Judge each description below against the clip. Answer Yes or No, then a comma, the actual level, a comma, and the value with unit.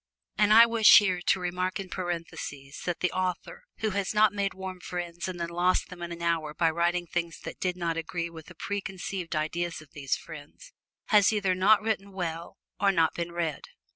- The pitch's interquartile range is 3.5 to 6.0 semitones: No, narrow, 2.4 semitones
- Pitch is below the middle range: No, medium, 180 Hz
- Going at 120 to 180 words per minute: No, average, 200 wpm